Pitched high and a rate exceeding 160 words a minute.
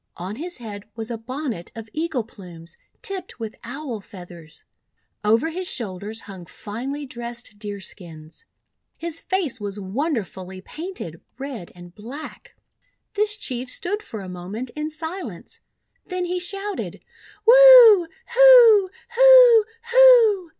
No: very high, 255 Hz; slow, 135 wpm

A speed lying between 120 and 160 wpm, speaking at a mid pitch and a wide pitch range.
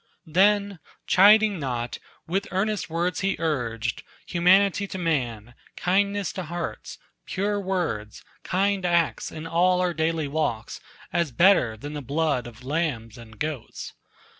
Yes: slow, 135 wpm; medium, 165 Hz; wide, 6.1 semitones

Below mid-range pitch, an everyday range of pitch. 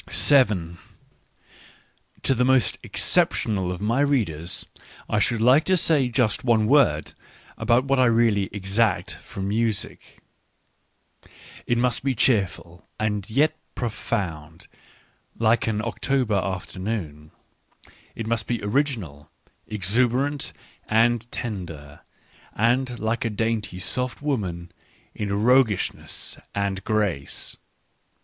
Yes: low, 110 Hz; average, 4.1 semitones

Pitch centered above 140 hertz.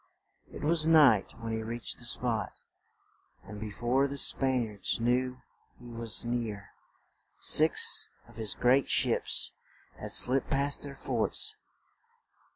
No: low, 120 Hz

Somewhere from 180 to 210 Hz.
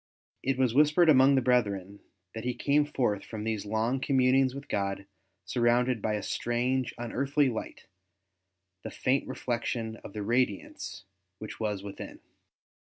No: low, 120 Hz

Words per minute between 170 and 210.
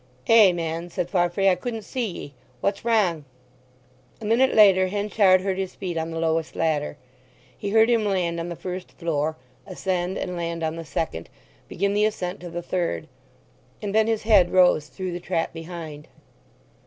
Yes: average, 180 wpm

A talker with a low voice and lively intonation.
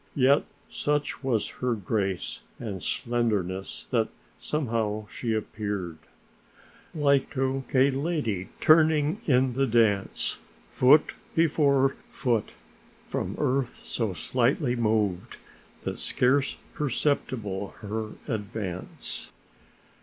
No: low, 120 Hz; average, 4.8 semitones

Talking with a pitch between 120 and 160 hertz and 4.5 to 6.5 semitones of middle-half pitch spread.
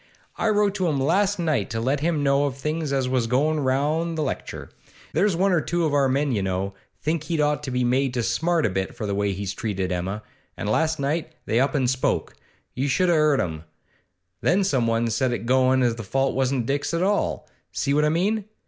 Yes: medium, 140 Hz; average, 5.0 semitones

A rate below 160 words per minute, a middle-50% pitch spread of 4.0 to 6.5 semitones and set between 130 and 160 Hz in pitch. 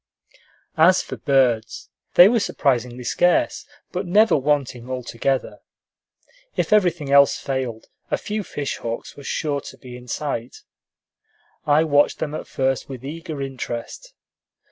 Yes: slow, 135 wpm; average, 4.5 semitones; medium, 140 Hz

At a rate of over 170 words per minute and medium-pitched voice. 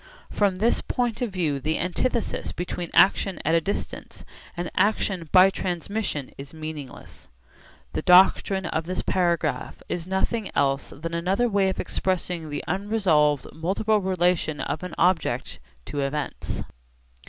No: average, 140 wpm; medium, 180 Hz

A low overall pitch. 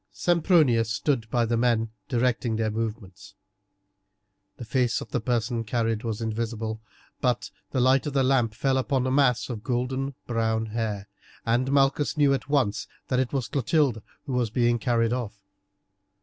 Yes: low, 120 Hz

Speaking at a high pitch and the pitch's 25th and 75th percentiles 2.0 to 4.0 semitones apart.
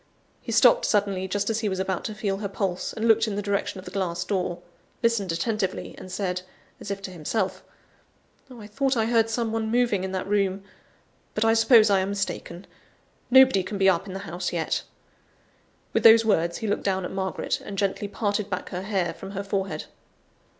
Yes: high, 200 Hz; narrow, 2.6 semitones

